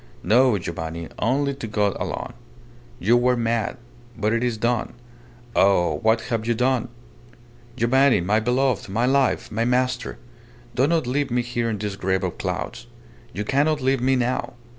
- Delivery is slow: No, average, 160 wpm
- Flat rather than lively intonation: No, average, 3.4 semitones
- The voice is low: Yes, low, 120 Hz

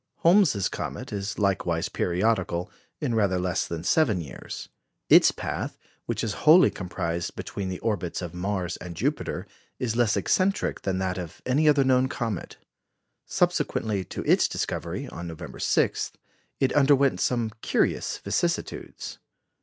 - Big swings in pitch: Yes, wide, 6.2 semitones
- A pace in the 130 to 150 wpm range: Yes, average, 140 wpm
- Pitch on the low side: Yes, low, 100 Hz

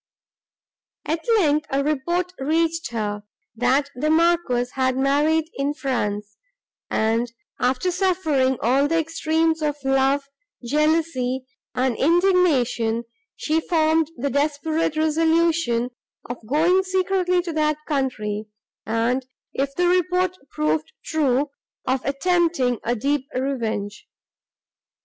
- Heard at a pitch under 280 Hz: No, very high, 290 Hz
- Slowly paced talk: Yes, slow, 110 wpm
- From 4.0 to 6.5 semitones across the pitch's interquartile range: Yes, average, 4.6 semitones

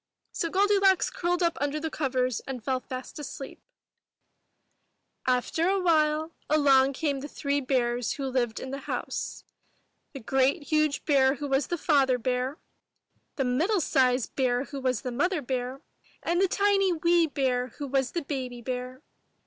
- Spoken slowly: No, average, 165 wpm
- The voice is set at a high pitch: Yes, very high, 275 Hz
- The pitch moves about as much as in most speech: Yes, average, 3.8 semitones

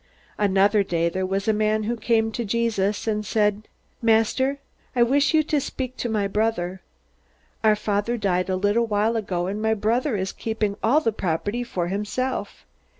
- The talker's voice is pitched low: No, high, 215 Hz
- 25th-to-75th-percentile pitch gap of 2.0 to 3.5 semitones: Yes, average, 2.7 semitones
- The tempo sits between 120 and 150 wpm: No, average, 175 wpm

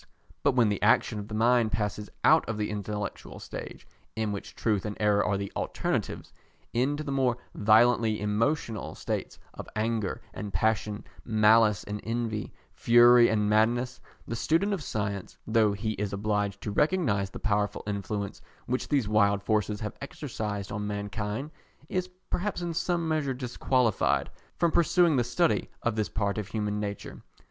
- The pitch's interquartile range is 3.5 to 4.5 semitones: No, average, 3.1 semitones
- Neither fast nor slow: Yes, average, 160 wpm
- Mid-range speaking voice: No, low, 110 Hz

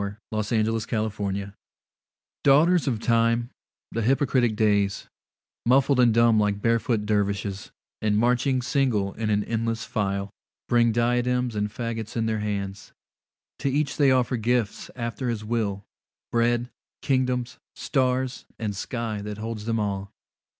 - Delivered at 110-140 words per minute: Yes, slow, 135 wpm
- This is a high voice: No, low, 115 Hz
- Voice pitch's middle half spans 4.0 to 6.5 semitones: No, average, 2.9 semitones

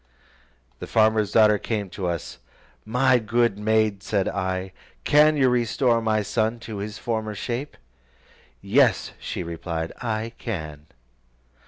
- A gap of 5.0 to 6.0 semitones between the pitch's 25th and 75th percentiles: No, average, 3.2 semitones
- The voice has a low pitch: Yes, low, 110 Hz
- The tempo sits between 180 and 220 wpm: No, slow, 135 wpm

